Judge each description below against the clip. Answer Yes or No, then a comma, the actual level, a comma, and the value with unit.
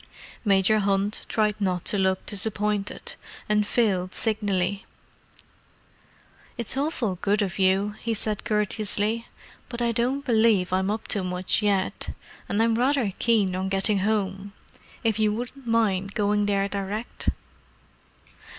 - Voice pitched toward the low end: No, high, 205 Hz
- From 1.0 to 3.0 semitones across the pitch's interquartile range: Yes, narrow, 2.4 semitones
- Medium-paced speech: No, slow, 130 wpm